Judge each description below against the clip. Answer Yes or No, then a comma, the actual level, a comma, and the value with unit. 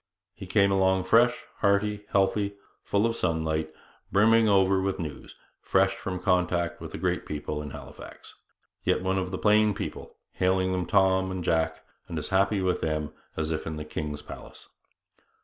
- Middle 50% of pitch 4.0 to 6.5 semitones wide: No, average, 3.3 semitones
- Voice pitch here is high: No, very low, 95 Hz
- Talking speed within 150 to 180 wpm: Yes, average, 170 wpm